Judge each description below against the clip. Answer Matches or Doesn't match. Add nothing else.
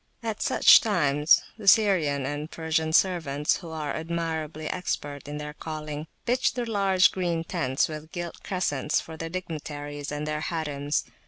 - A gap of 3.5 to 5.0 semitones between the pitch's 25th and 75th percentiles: Doesn't match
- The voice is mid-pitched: Matches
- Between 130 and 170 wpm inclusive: Matches